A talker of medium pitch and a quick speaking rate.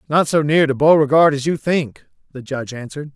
Yes: medium, 145 Hz; fast, 230 wpm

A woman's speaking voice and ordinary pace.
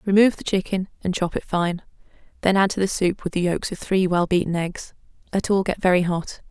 No: female; fast, 230 wpm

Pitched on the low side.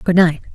No: medium, 170 Hz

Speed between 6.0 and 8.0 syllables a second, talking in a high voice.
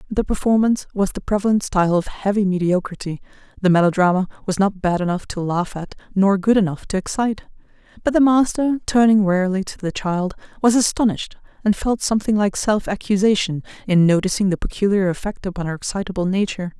Yes: 6.1 syllables/s; high, 195 Hz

